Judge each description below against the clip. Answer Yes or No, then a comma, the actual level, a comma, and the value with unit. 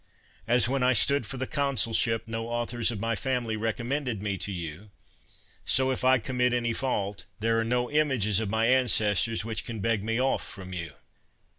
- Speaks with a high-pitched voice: No, low, 115 Hz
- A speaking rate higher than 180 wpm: Yes, average, 190 wpm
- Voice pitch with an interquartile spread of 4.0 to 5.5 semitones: No, average, 2.8 semitones